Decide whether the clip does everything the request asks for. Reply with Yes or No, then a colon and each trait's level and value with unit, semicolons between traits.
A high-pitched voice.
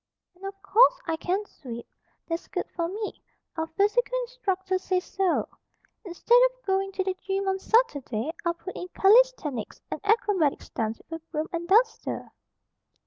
Yes: very high, 380 Hz